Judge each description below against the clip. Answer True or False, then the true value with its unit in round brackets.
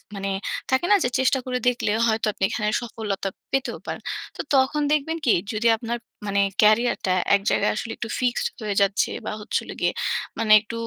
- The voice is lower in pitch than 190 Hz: False (230 Hz)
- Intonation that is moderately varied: True (3.2 semitones)